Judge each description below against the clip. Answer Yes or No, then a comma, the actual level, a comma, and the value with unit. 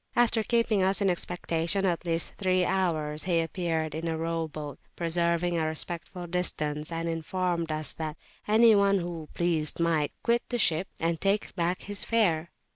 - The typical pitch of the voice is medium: Yes, medium, 170 Hz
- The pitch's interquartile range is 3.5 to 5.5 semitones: No, average, 2.8 semitones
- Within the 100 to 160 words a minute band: No, average, 170 wpm